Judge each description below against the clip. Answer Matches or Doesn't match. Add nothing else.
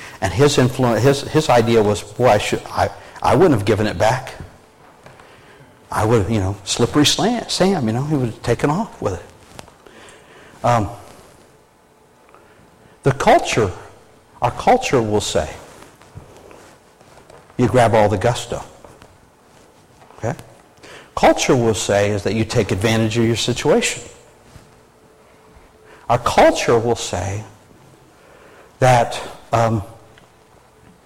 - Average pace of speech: Doesn't match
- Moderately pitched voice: Doesn't match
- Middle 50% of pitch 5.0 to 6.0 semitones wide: Doesn't match